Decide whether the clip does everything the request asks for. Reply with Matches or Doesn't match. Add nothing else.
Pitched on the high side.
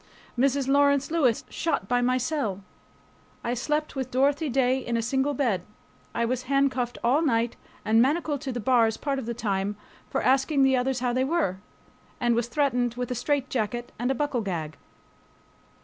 Matches